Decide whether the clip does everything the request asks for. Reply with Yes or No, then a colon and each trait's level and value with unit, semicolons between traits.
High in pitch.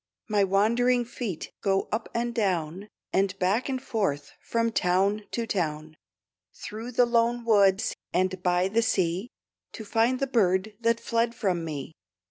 Yes: high, 210 Hz